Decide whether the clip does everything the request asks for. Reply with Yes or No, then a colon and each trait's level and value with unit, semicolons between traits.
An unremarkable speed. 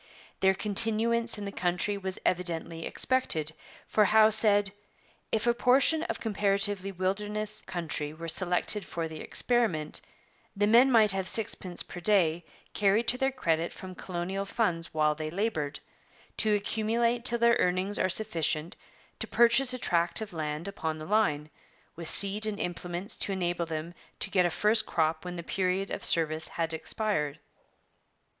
Yes: average, 160 wpm